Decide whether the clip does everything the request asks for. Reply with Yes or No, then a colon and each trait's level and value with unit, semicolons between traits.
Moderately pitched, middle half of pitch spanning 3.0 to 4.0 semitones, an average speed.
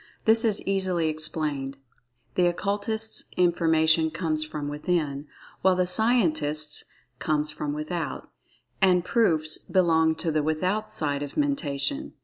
No: medium, 160 Hz; average, 3.7 semitones; slow, 115 wpm